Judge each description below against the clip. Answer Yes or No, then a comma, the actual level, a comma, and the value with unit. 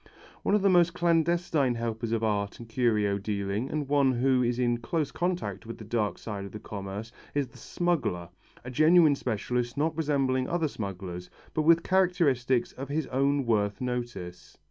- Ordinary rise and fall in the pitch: No, wide, 6.1 semitones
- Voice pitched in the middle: No, low, 125 Hz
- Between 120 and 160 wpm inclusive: No, average, 175 wpm